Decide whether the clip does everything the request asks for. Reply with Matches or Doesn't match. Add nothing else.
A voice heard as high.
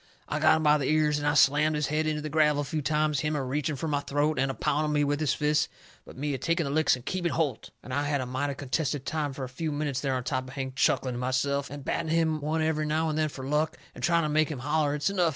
Doesn't match